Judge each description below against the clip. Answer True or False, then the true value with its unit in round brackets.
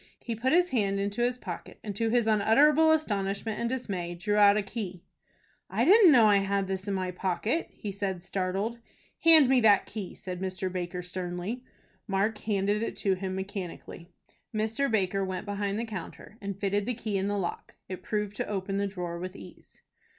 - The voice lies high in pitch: True (200 Hz)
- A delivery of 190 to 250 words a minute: True (195 wpm)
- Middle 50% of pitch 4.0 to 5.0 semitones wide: False (2.9 semitones)